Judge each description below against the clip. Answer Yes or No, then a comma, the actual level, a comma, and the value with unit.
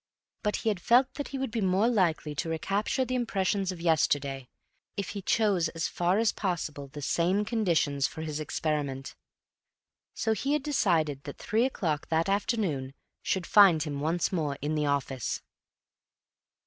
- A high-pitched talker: No, medium, 175 Hz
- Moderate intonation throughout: No, wide, 5.9 semitones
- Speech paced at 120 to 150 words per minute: No, average, 165 wpm